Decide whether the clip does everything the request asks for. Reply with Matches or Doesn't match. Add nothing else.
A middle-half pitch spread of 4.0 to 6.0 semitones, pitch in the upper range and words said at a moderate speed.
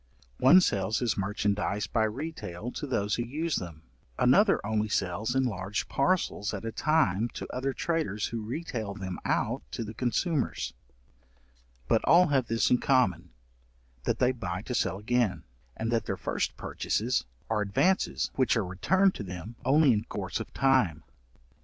Doesn't match